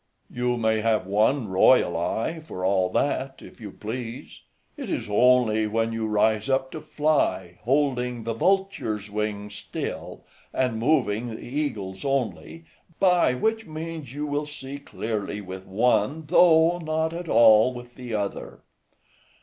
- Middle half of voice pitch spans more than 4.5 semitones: Yes, wide, 5.5 semitones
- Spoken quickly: No, average, 145 wpm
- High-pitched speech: No, low, 120 Hz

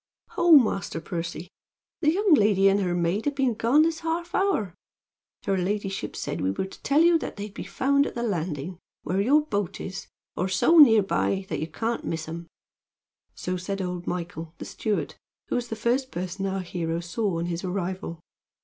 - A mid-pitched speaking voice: No, high, 195 Hz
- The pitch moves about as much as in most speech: No, wide, 5.8 semitones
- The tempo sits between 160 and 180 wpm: No, average, 195 wpm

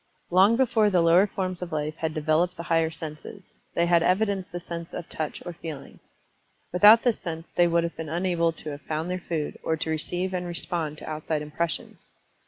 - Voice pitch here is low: No, medium, 170 Hz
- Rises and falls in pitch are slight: Yes, narrow, 2.3 semitones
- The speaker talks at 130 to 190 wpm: No, average, 200 wpm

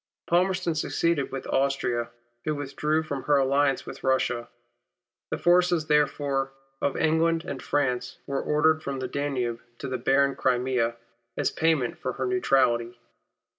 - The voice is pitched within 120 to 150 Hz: Yes, medium, 140 Hz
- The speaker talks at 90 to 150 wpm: Yes, average, 140 wpm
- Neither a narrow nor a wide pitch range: Yes, average, 3.3 semitones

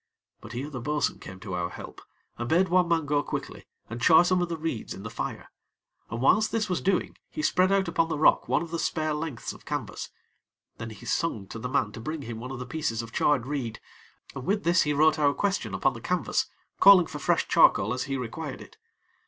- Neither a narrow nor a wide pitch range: No, wide, 6.0 semitones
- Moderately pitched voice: Yes, medium, 150 Hz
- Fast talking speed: Yes, fast, 235 wpm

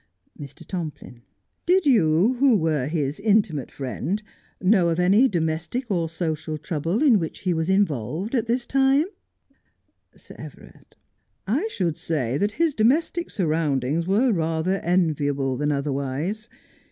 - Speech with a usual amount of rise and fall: No, wide, 6.1 semitones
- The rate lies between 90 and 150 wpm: Yes, average, 140 wpm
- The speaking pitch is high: No, medium, 170 Hz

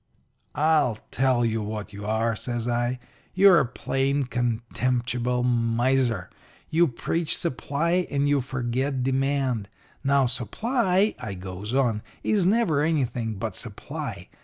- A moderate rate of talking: No, slow, 125 wpm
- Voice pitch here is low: Yes, low, 125 Hz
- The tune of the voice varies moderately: Yes, average, 3.6 semitones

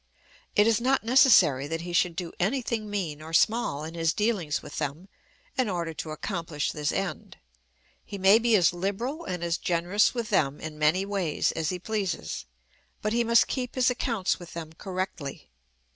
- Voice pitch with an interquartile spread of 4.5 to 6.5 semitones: Yes, average, 5.1 semitones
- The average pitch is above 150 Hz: Yes, medium, 185 Hz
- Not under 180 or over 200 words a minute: Yes, average, 185 wpm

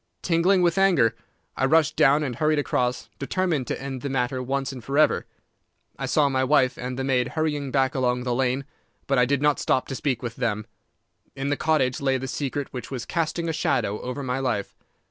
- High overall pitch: No, low, 135 Hz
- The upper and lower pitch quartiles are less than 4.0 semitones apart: Yes, average, 2.9 semitones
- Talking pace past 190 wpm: Yes, fast, 205 wpm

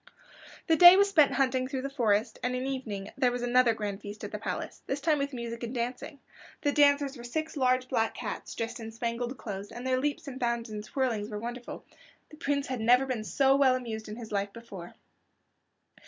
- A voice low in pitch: No, very high, 250 Hz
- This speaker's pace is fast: Yes, fast, 220 wpm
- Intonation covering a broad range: No, average, 3.3 semitones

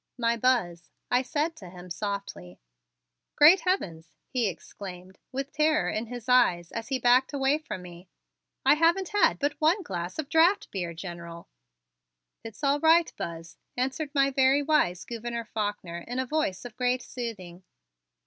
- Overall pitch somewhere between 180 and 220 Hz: No, high, 240 Hz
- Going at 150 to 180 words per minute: Yes, average, 160 wpm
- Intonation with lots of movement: Yes, wide, 8.1 semitones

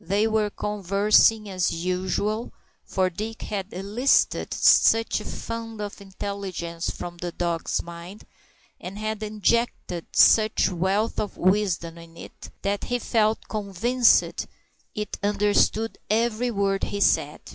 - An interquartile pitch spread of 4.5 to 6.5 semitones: No, average, 2.8 semitones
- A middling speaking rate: No, slow, 125 wpm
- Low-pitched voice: No, high, 205 Hz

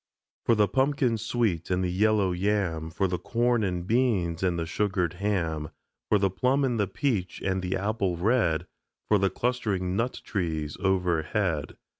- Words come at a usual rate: Yes, average, 165 wpm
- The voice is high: No, very low, 95 Hz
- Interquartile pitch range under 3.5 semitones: No, average, 3.9 semitones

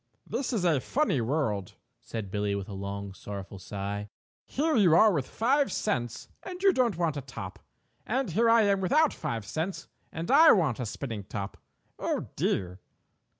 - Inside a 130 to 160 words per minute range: No, average, 180 wpm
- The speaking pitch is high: No, medium, 145 Hz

